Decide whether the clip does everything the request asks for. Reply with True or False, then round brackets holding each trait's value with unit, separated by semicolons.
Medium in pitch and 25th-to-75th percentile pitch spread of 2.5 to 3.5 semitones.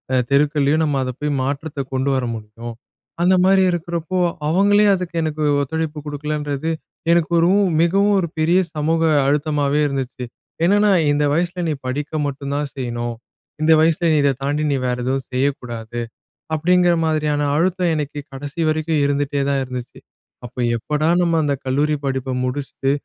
True (150 Hz; 3.2 semitones)